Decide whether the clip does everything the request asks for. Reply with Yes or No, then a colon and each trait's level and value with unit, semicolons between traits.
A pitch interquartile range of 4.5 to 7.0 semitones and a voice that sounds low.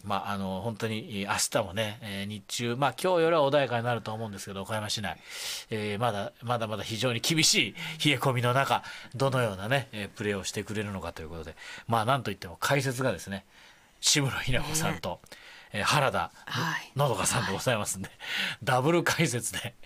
Yes: average, 5.2 semitones; low, 115 Hz